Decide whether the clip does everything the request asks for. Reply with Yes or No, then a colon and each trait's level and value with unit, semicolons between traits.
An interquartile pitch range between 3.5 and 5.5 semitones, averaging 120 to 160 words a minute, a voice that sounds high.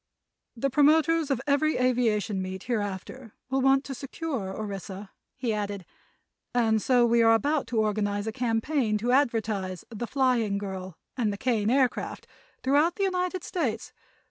Yes: average, 4.7 semitones; average, 150 wpm; high, 235 Hz